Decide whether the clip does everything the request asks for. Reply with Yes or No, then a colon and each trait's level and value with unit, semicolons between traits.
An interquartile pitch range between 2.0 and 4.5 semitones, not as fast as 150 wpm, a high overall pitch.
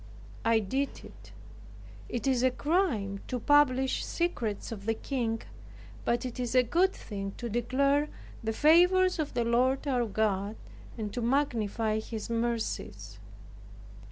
Yes: average, 3.9 semitones; average, 140 wpm; high, 240 Hz